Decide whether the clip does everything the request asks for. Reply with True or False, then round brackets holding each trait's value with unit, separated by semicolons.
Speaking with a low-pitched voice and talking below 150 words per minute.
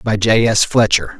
False (110 Hz; 200 wpm)